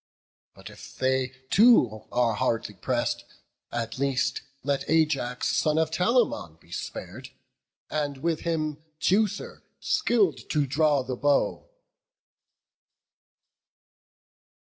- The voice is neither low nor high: Yes, medium, 145 Hz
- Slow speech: Yes, slow, 100 wpm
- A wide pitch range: No, average, 4.4 semitones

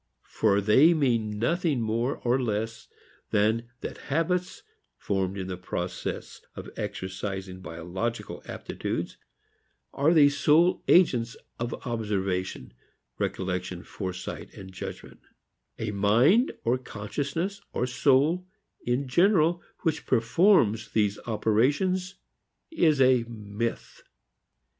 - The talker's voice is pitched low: Yes, low, 115 Hz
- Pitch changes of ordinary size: No, wide, 6.6 semitones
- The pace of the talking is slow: Yes, slow, 100 wpm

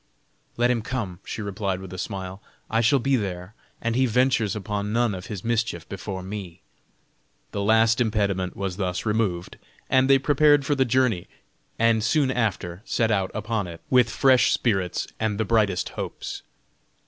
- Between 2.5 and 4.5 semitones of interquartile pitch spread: Yes, average, 3.9 semitones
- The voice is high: No, low, 110 Hz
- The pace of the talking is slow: No, average, 165 wpm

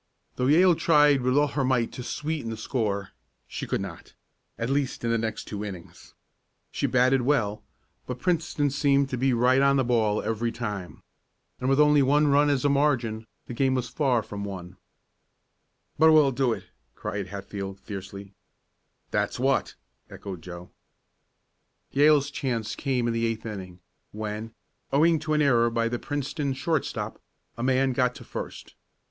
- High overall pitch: No, low, 125 Hz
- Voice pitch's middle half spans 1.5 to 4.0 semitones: No, average, 4.4 semitones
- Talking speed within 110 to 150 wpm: No, average, 165 wpm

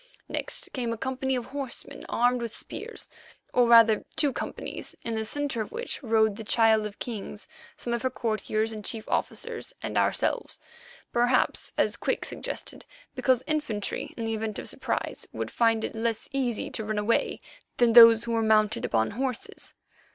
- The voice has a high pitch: Yes, high, 230 Hz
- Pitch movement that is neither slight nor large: No, narrow, 2.3 semitones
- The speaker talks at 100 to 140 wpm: No, average, 175 wpm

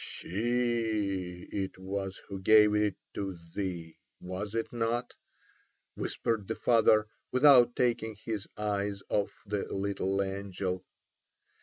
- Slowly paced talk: Yes, slow, 115 wpm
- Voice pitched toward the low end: Yes, low, 105 Hz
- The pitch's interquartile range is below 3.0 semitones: Yes, narrow, 2.6 semitones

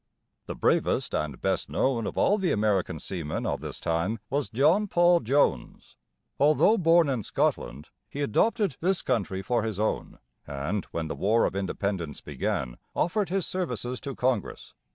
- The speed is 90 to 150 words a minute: No, average, 160 wpm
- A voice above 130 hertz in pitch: No, low, 115 Hz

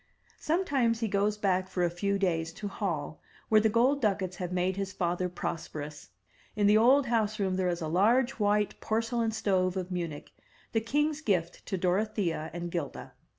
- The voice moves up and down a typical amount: Yes, average, 3.8 semitones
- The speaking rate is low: No, average, 185 wpm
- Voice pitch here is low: No, high, 195 Hz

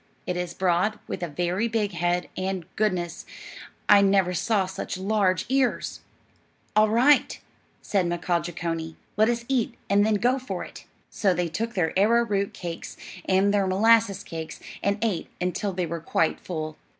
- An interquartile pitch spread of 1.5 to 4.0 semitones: Yes, average, 3.5 semitones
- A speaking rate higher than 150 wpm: Yes, average, 160 wpm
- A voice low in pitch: No, high, 190 Hz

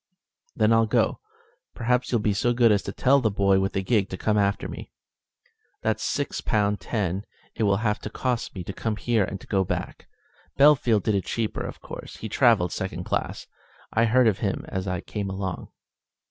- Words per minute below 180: No, average, 195 wpm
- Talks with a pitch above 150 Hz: No, low, 105 Hz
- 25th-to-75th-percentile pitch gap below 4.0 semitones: Yes, average, 3.0 semitones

